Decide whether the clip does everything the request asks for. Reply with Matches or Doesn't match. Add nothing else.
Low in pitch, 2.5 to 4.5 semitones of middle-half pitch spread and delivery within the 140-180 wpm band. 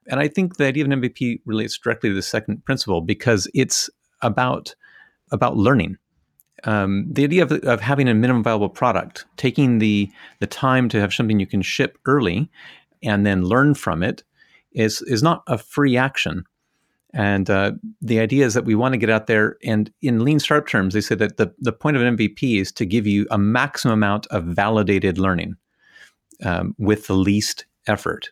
Doesn't match